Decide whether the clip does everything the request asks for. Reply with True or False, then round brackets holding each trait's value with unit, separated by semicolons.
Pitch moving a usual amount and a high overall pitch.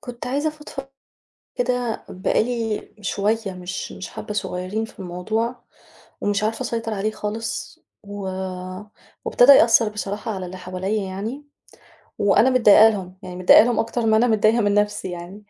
True (3.0 semitones; 215 Hz)